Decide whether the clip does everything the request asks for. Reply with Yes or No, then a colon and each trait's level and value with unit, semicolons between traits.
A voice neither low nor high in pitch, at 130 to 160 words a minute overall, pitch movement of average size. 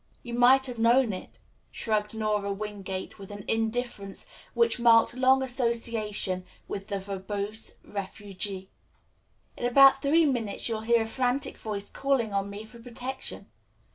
No: high, 225 Hz; average, 140 wpm; average, 3.5 semitones